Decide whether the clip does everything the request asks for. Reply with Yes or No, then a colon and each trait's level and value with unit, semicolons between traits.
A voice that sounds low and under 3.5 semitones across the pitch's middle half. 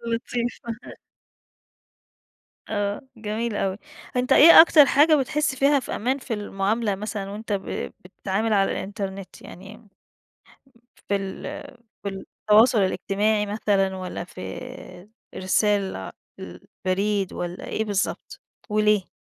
No: high, 210 Hz; average, 3.1 semitones